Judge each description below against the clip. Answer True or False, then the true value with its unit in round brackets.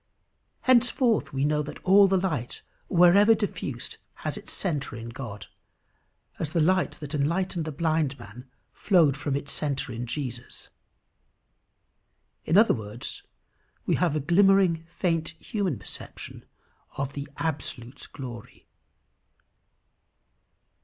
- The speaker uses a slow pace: True (120 wpm)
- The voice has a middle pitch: True (155 Hz)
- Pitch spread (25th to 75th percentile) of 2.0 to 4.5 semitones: False (5.3 semitones)